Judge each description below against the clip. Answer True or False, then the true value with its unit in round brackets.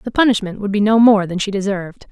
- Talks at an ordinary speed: False (255 wpm)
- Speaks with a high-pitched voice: True (205 Hz)